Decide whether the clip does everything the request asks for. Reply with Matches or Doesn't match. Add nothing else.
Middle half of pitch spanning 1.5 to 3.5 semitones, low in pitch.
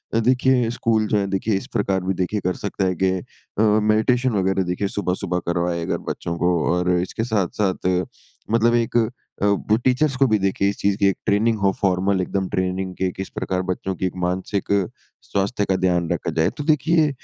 Matches